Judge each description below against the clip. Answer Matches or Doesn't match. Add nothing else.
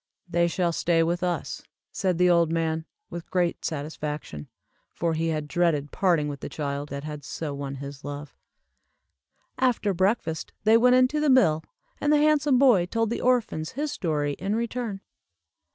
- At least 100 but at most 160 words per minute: Doesn't match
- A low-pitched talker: Doesn't match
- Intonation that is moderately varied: Doesn't match